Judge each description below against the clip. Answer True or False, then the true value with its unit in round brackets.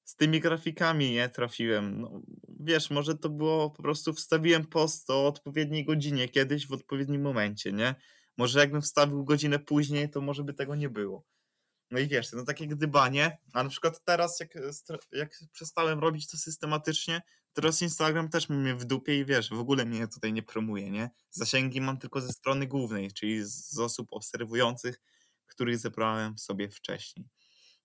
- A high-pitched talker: False (140 Hz)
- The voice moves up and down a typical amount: True (4.2 semitones)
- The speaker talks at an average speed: False (170 wpm)